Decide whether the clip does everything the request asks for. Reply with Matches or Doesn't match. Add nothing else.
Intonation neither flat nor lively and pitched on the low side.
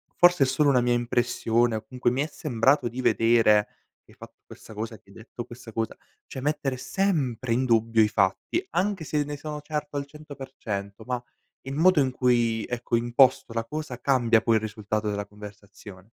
Matches